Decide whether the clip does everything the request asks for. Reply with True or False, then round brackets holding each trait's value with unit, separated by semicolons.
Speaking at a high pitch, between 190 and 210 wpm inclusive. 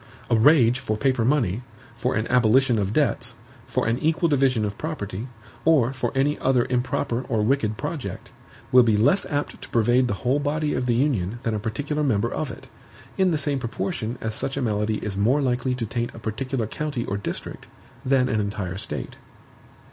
False (125 Hz; 195 wpm)